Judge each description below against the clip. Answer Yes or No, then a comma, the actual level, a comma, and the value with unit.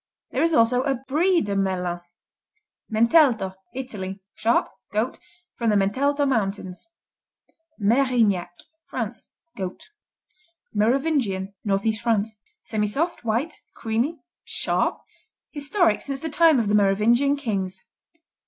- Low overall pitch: No, high, 225 Hz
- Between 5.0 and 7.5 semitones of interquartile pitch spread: Yes, wide, 5.5 semitones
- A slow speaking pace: Yes, slow, 105 wpm